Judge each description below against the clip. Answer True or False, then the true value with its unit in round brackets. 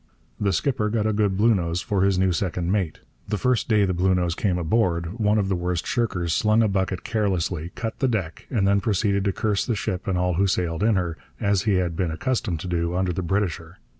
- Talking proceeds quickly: True (225 wpm)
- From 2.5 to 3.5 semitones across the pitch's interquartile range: True (3.1 semitones)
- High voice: False (95 Hz)